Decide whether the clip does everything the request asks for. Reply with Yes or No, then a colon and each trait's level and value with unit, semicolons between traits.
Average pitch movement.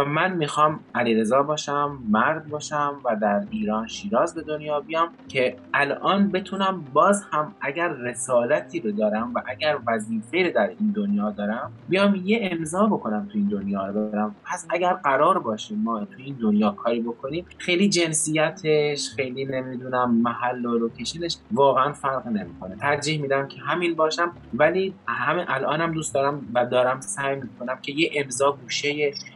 No: wide, 5.8 semitones